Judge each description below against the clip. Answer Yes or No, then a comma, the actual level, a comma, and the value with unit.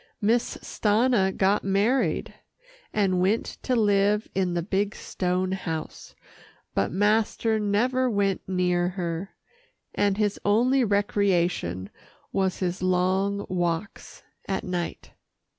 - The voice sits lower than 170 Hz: No, high, 195 Hz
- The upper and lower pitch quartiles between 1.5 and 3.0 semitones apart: Yes, narrow, 2.4 semitones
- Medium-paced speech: No, slow, 110 wpm